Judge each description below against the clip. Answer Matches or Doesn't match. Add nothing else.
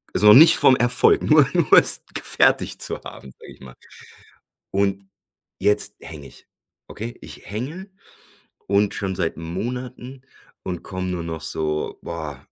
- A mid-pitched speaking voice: Doesn't match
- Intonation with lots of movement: Matches